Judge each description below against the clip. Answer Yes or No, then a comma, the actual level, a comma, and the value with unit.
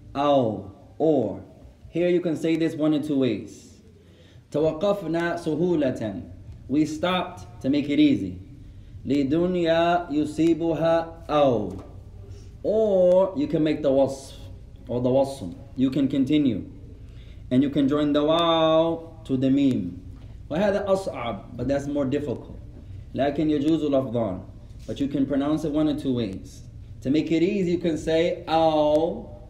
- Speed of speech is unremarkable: No, slow, 125 wpm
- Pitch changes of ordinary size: No, wide, 7.0 semitones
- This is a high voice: No, medium, 140 Hz